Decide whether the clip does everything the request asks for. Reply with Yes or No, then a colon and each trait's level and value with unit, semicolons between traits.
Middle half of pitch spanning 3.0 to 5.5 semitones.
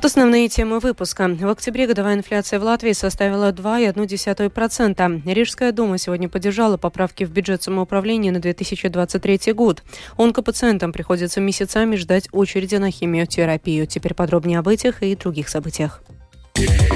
Yes: average, 3.5 semitones